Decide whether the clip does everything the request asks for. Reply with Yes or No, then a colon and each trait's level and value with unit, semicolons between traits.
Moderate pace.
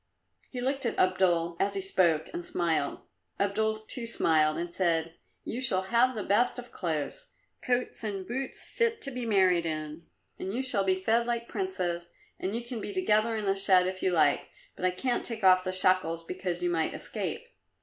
Yes: average, 195 wpm